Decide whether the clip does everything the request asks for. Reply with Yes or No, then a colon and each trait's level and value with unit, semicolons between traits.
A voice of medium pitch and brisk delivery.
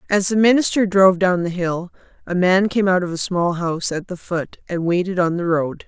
Yes: medium, 180 Hz; fast, 235 wpm